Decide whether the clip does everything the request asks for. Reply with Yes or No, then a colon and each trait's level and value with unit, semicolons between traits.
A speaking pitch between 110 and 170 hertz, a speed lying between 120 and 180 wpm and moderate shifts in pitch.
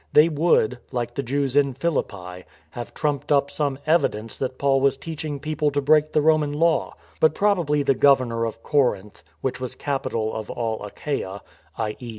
No: medium, 140 Hz; average, 190 wpm; average, 4.2 semitones